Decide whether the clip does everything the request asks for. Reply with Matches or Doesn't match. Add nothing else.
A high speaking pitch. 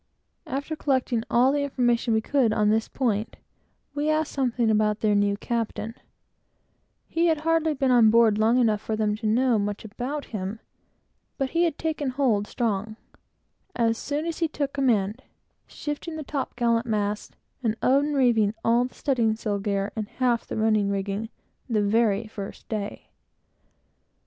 Matches